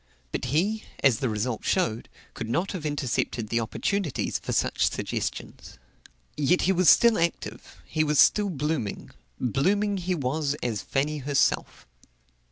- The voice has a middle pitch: Yes, medium, 150 Hz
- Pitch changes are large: Yes, wide, 6.4 semitones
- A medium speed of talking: Yes, average, 145 wpm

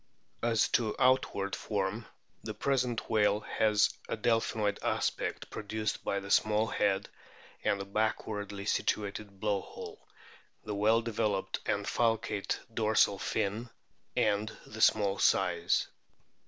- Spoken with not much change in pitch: Yes, narrow, 1.7 semitones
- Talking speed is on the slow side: Yes, slow, 125 wpm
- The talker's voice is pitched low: Yes, low, 105 Hz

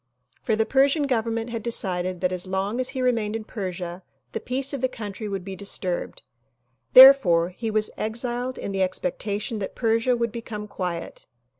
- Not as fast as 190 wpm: Yes, average, 175 wpm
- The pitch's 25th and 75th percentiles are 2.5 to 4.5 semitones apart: Yes, average, 4.2 semitones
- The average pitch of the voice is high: Yes, high, 215 Hz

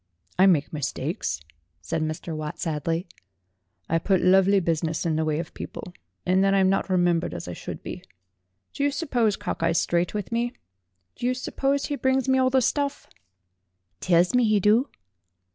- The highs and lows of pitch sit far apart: Yes, wide, 6.8 semitones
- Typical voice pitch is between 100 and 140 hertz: No, high, 190 Hz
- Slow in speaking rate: No, average, 180 wpm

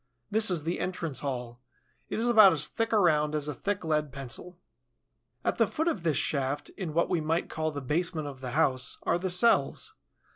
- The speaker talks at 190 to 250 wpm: Yes, fast, 205 wpm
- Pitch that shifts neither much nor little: Yes, average, 4.2 semitones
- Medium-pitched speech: Yes, medium, 160 Hz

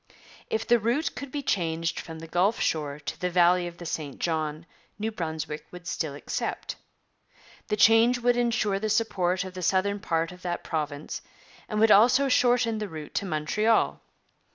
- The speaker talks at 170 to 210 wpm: Yes, average, 175 wpm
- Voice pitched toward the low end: No, medium, 185 Hz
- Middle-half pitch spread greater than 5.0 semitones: Yes, wide, 5.5 semitones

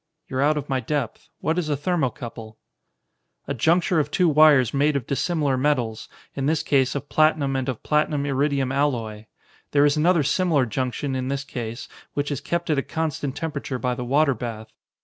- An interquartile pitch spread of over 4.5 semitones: No, average, 2.9 semitones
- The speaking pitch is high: No, medium, 140 Hz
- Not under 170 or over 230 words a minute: Yes, average, 190 wpm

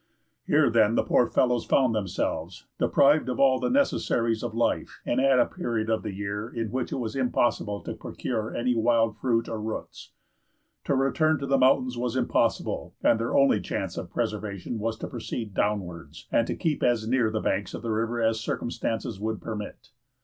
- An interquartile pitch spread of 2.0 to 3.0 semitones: Yes, average, 2.7 semitones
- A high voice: No, low, 115 Hz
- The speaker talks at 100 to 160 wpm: No, average, 190 wpm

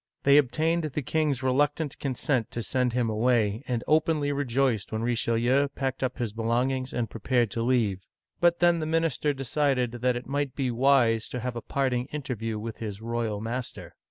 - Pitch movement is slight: No, average, 3.4 semitones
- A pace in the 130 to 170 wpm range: No, average, 185 wpm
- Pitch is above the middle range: No, low, 125 Hz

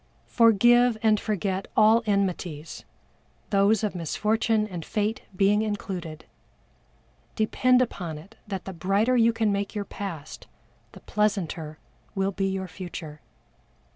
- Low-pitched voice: No, high, 200 Hz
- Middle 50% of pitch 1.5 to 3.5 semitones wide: Yes, average, 3.0 semitones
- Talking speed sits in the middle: No, slow, 125 wpm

